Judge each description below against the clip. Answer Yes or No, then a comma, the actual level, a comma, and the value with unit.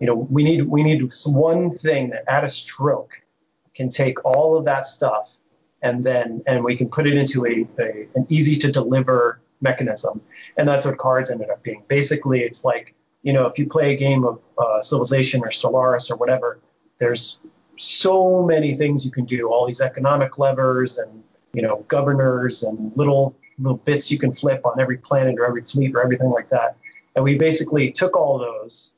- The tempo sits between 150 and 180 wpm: No, average, 200 wpm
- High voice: No, low, 130 Hz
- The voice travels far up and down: No, average, 2.9 semitones